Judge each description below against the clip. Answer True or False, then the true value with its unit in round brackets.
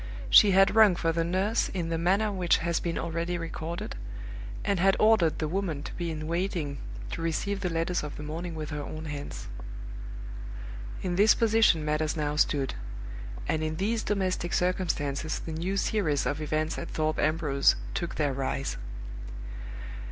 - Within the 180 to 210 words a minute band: False (165 wpm)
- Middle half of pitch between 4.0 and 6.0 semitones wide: False (3.4 semitones)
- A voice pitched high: False (165 Hz)